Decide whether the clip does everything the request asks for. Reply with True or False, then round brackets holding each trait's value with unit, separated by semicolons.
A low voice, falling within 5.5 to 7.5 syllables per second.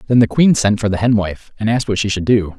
True (105 Hz; 6.4 syllables/s)